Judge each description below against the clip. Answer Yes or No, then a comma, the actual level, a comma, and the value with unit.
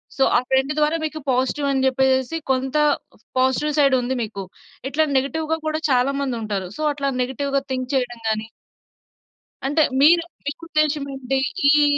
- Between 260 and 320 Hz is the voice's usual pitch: Yes, very high, 270 Hz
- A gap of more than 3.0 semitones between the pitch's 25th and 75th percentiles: No, narrow, 2.5 semitones